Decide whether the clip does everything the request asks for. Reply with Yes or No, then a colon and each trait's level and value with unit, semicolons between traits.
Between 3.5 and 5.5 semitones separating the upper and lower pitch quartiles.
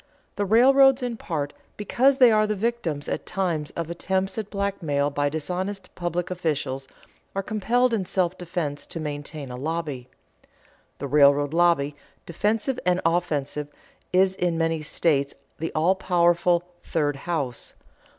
Yes: average, 4.9 semitones